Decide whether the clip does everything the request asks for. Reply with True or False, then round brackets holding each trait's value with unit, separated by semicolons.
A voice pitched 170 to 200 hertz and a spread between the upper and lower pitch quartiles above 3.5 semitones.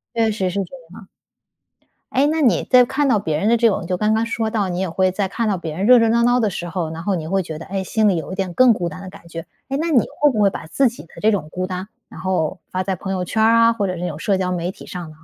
True (195 Hz; 4.2 semitones)